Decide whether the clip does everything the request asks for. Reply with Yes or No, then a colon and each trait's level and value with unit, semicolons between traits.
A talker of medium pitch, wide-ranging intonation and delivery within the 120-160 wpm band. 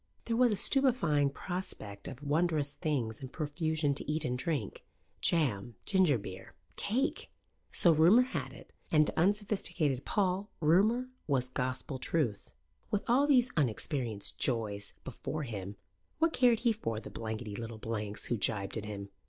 Yes: medium, 150 Hz; wide, 8.8 semitones; average, 150 wpm